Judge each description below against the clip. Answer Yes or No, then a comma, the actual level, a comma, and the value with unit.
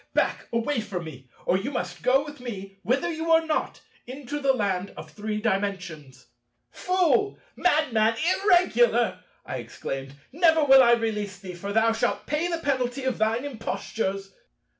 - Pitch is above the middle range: Yes, high, 230 Hz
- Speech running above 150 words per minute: No, average, 145 wpm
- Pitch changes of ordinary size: No, wide, 6.9 semitones